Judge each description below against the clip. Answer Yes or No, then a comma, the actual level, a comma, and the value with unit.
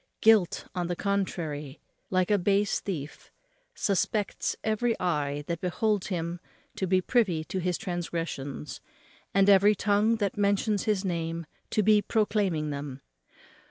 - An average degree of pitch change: Yes, average, 3.7 semitones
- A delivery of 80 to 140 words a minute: Yes, slow, 135 wpm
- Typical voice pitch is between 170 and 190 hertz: Yes, medium, 185 Hz